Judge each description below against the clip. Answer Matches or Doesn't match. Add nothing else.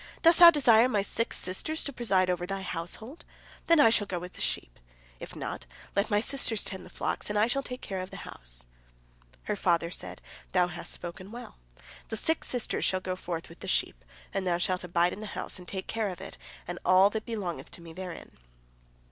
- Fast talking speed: Matches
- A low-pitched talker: Doesn't match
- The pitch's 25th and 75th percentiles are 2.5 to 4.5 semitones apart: Matches